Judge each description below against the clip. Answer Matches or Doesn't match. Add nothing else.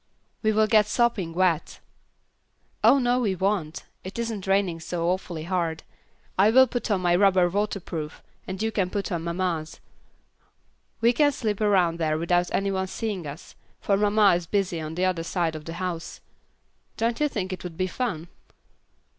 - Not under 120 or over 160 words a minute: Doesn't match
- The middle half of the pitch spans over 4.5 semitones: Doesn't match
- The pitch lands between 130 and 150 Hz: Doesn't match